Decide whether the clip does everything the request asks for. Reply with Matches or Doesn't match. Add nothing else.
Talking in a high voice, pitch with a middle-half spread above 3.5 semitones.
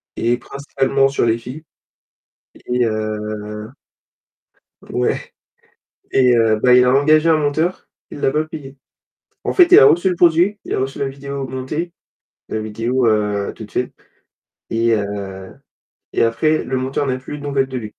Doesn't match